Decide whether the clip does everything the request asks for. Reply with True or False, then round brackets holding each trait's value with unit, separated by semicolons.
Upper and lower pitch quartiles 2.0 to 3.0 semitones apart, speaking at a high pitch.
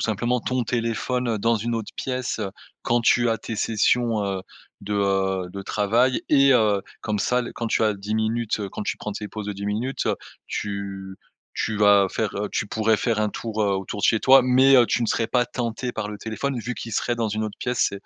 False (2.7 semitones; 110 Hz)